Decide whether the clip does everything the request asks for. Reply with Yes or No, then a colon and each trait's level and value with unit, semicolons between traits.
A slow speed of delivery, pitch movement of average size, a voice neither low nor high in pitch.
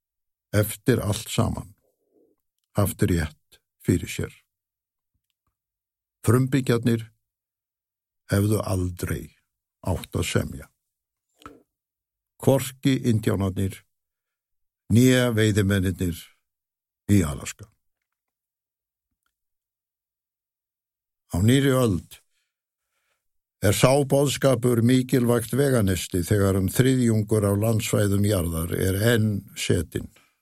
No: slow, 70 wpm; average, 3.8 semitones; low, 105 Hz